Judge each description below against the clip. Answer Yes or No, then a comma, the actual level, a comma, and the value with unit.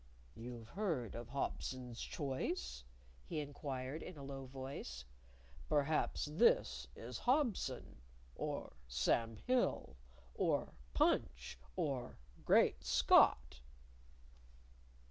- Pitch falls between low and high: No, low, 130 Hz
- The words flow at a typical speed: No, slow, 90 wpm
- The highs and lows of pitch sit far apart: No, average, 4.8 semitones